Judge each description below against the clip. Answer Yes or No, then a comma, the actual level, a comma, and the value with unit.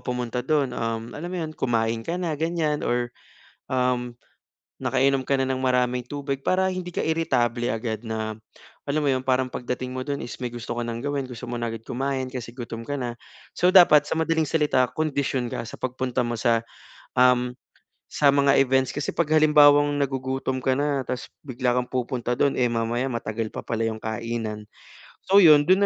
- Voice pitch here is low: Yes, low, 130 Hz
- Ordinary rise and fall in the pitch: Yes, average, 3.3 semitones